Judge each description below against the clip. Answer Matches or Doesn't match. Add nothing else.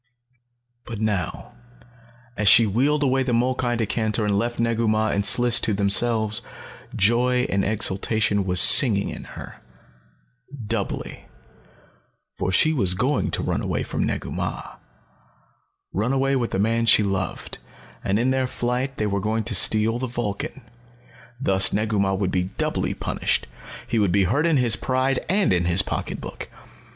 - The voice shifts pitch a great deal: Doesn't match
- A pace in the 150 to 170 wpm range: Matches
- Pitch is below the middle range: Matches